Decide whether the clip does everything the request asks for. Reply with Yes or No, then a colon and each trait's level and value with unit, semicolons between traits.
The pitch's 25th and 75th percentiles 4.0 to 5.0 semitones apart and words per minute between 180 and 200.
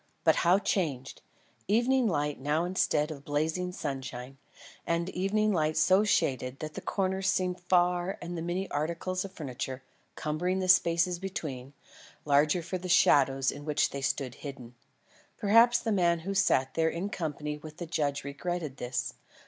No: average, 4.3 semitones; average, 160 wpm